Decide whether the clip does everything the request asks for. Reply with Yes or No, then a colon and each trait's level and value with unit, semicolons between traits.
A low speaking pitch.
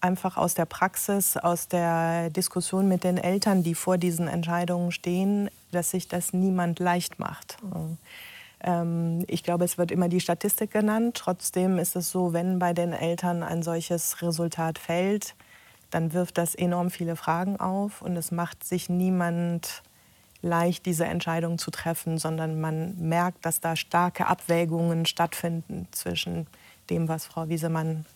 No: medium, 175 Hz